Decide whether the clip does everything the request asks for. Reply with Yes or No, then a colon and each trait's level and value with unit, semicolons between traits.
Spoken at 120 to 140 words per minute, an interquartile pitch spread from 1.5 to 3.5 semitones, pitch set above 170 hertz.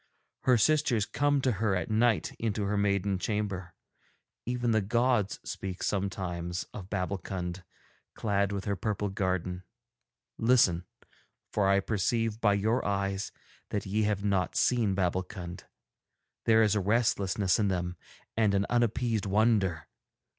No: slow, 135 wpm; average, 2.8 semitones; low, 100 Hz